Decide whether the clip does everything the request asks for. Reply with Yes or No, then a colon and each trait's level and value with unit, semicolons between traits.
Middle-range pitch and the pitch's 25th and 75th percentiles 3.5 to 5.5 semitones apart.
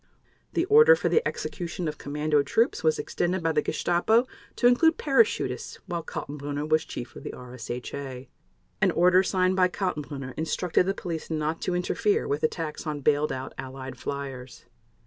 Yes: medium, 155 Hz; average, 4.6 semitones